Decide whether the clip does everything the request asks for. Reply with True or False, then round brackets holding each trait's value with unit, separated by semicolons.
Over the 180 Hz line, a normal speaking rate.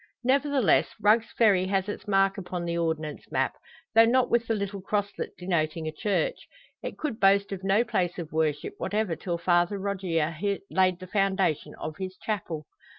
True (190 Hz; 170 wpm)